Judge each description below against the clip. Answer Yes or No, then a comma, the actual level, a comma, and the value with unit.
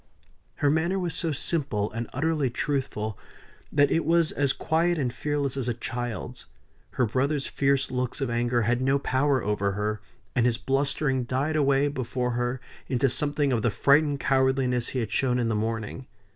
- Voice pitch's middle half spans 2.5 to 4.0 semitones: Yes, average, 3.1 semitones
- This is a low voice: Yes, low, 130 Hz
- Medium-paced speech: Yes, average, 175 wpm